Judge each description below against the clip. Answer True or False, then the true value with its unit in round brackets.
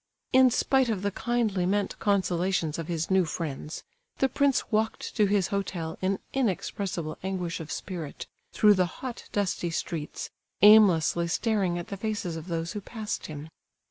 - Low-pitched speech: False (190 Hz)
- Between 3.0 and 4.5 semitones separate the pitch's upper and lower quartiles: True (4.0 semitones)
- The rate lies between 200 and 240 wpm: False (160 wpm)